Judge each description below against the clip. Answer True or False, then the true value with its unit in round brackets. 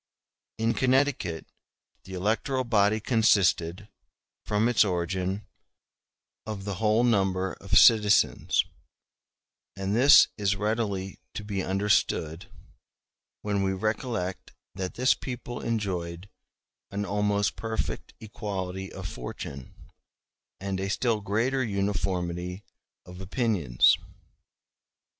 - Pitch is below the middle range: True (100 Hz)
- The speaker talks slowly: True (100 wpm)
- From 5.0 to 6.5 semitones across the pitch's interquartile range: False (2.9 semitones)